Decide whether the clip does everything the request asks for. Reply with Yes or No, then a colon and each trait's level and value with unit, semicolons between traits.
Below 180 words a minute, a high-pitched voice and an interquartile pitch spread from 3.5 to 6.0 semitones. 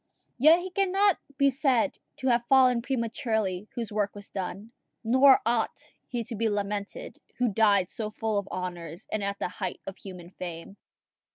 Yes: average, 170 wpm; high, 220 Hz; average, 4.3 semitones